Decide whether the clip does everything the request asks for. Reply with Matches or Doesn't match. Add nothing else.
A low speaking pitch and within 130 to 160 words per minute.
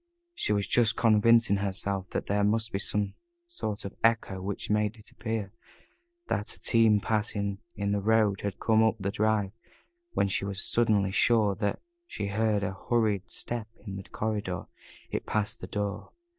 Doesn't match